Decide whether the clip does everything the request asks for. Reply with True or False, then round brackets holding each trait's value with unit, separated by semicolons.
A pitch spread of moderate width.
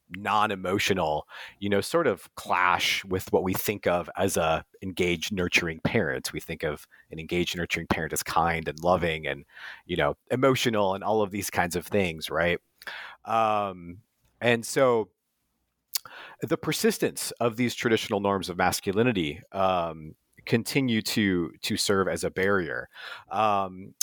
True (4.2 semitones)